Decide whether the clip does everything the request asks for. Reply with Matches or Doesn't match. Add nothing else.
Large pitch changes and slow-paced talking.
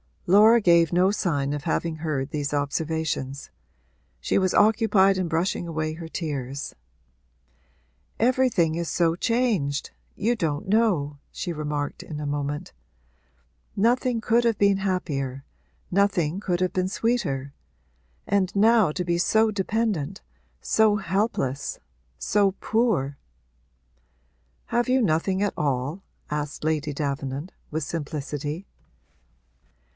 Matches